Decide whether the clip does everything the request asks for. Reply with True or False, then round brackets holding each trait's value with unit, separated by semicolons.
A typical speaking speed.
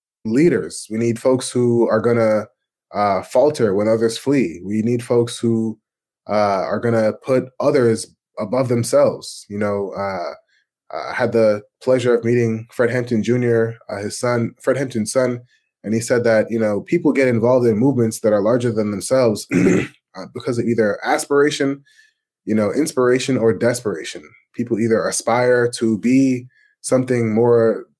True (160 wpm)